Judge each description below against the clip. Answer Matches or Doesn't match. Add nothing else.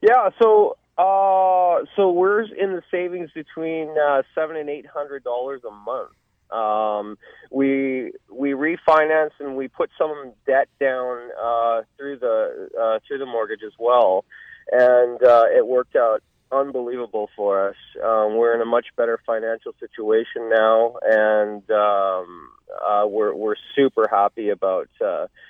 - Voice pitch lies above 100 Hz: Matches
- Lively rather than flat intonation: Matches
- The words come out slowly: Doesn't match